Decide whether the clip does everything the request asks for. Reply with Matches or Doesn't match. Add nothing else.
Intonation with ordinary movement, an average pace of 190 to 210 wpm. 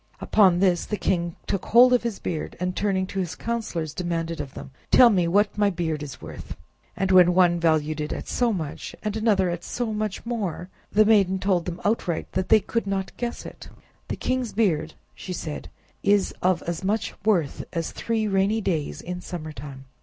Matches